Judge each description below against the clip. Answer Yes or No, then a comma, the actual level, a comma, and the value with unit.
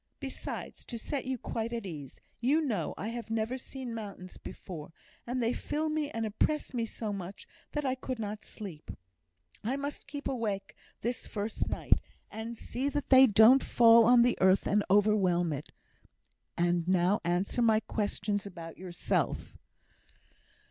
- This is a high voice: Yes, high, 220 Hz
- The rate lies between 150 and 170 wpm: Yes, average, 160 wpm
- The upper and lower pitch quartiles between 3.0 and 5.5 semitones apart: Yes, average, 4.4 semitones